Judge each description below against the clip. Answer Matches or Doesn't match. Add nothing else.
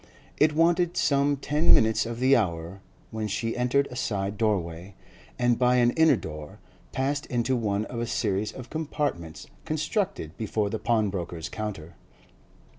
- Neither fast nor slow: Matches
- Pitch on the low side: Matches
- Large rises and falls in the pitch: Matches